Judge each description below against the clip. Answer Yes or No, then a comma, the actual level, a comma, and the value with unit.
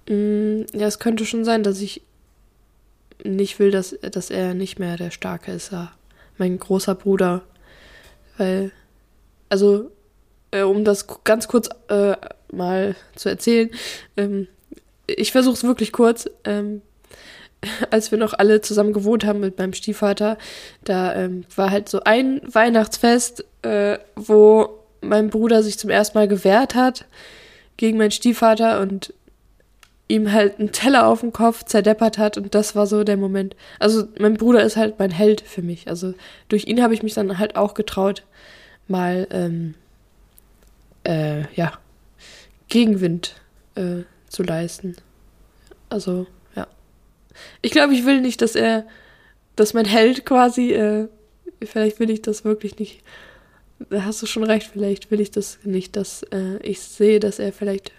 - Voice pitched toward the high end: Yes, high, 210 Hz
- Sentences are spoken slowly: No, average, 150 wpm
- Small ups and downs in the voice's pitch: Yes, narrow, 2.2 semitones